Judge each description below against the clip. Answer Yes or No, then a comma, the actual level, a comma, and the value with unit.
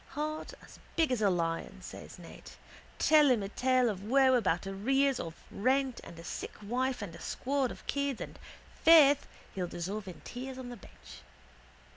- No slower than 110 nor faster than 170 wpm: No, average, 180 wpm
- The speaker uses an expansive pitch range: Yes, wide, 5.8 semitones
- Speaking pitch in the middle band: No, very high, 250 Hz